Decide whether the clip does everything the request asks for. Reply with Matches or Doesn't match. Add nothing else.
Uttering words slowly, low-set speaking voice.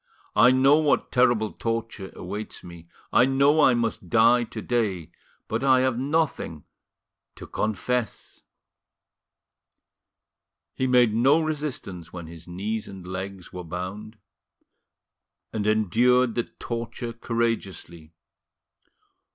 Matches